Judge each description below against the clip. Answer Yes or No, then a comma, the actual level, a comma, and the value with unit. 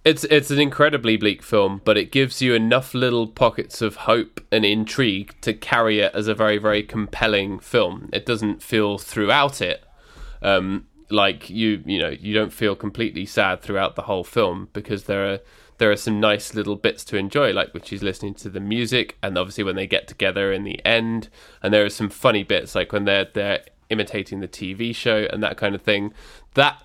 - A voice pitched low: Yes, low, 105 Hz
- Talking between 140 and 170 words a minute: No, fast, 205 wpm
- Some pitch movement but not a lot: No, narrow, 2.3 semitones